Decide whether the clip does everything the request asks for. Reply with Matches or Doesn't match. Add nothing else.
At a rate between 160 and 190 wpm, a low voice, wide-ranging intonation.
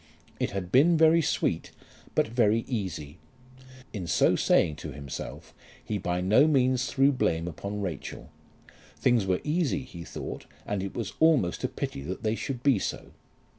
Matches